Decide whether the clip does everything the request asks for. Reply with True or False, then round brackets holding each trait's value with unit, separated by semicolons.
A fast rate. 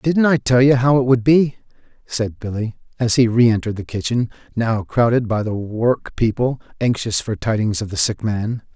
False (185 wpm)